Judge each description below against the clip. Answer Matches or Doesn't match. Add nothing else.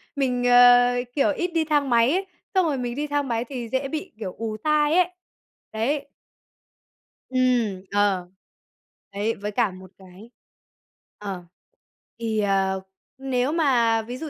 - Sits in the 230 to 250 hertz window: Matches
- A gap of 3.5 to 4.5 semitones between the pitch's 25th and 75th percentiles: Doesn't match